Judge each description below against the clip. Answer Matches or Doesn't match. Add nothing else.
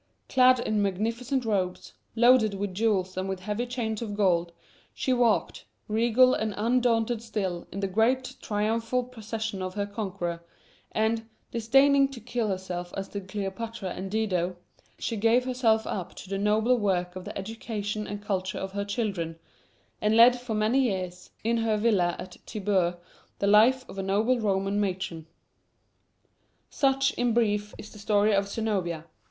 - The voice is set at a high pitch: Matches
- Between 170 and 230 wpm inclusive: Doesn't match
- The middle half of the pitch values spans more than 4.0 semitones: Doesn't match